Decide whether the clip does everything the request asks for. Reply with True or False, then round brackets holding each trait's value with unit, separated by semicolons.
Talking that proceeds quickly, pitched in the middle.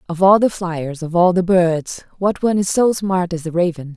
True (240 wpm; 180 Hz)